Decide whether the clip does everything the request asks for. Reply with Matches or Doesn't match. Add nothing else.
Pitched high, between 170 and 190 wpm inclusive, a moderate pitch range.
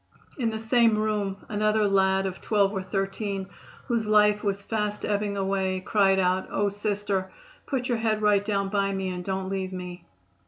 Doesn't match